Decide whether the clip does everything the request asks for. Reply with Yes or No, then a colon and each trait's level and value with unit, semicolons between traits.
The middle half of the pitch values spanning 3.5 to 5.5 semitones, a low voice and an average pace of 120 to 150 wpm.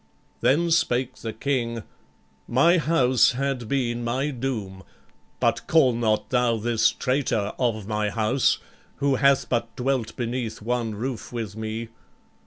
No: average, 3.0 semitones; low, 120 Hz; slow, 135 wpm